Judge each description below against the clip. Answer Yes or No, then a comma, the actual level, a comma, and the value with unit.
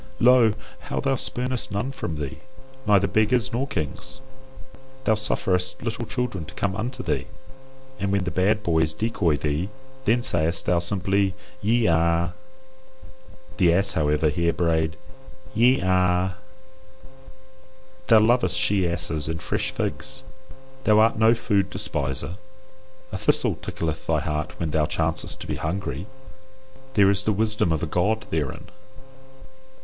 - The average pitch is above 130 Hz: No, very low, 95 Hz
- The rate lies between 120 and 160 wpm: Yes, average, 140 wpm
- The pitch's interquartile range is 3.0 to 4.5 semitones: No, average, 5.0 semitones